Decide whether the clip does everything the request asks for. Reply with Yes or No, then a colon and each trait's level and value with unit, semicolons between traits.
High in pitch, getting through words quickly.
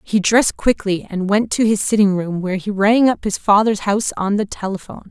Yes: high, 205 Hz; fast, 225 wpm